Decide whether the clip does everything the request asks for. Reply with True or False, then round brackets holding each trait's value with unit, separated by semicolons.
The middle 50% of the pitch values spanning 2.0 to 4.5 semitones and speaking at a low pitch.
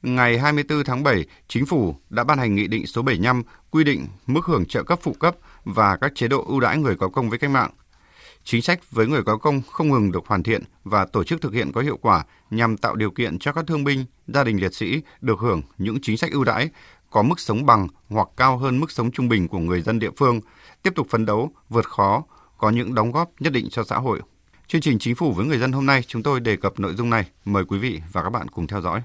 False (5.2 semitones; 120 Hz)